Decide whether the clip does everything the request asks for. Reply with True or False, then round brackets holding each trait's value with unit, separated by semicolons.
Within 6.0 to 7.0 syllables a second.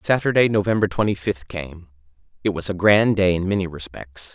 False (5.5 syllables/s)